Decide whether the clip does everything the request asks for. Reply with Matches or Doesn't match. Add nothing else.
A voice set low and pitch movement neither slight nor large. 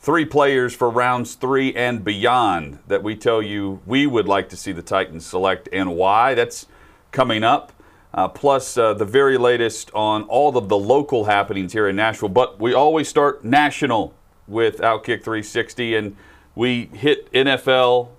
Matches